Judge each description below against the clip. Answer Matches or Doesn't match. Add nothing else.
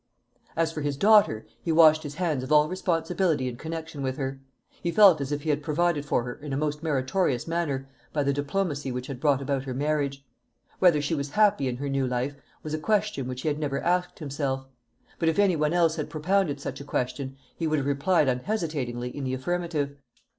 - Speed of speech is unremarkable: Doesn't match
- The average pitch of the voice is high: Doesn't match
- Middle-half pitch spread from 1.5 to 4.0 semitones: Matches